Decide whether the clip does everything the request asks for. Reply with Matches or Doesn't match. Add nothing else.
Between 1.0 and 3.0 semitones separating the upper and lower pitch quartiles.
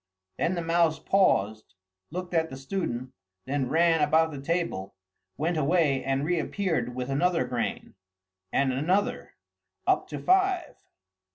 Doesn't match